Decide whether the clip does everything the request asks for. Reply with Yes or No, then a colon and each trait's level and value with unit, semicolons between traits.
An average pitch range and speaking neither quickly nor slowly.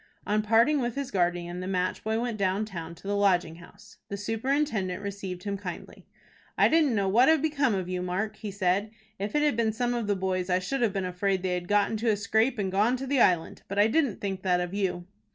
No: average, 3.8 semitones; fast, 240 wpm